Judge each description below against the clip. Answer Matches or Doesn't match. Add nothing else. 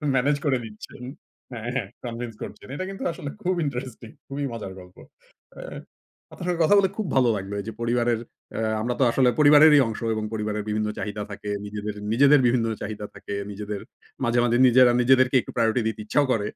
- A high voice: Doesn't match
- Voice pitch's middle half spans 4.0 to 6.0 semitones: Matches